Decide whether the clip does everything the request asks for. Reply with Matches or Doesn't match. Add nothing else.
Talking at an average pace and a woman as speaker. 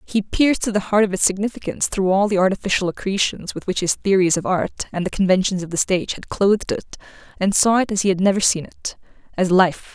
Doesn't match